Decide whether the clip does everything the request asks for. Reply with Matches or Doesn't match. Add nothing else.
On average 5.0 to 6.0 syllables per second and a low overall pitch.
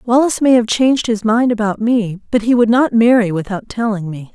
Doesn't match